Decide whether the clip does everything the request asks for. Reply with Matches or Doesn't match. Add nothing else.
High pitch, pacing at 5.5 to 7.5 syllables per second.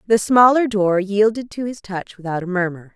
Doesn't match